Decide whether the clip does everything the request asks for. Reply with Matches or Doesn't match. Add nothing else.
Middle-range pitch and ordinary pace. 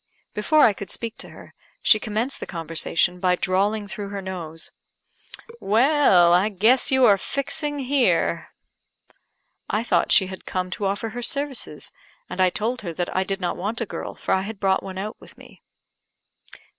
Doesn't match